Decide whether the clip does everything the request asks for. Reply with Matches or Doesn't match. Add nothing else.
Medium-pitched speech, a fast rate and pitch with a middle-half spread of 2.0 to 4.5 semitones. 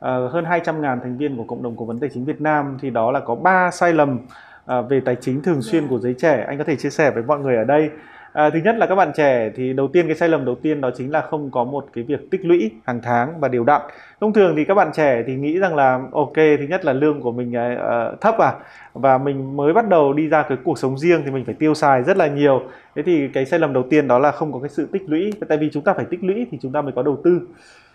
Matches